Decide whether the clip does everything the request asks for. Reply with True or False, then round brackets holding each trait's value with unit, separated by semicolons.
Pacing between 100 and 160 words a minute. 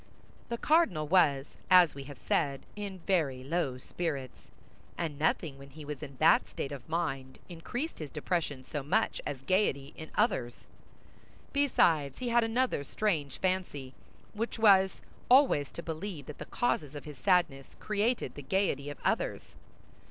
True (155 wpm)